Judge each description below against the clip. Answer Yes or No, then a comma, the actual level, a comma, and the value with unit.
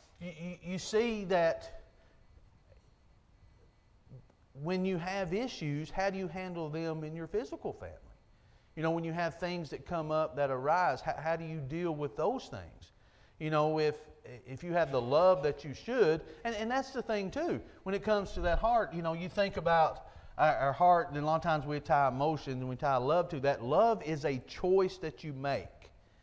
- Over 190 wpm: Yes, average, 200 wpm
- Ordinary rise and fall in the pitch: Yes, average, 4.8 semitones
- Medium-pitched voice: Yes, medium, 160 Hz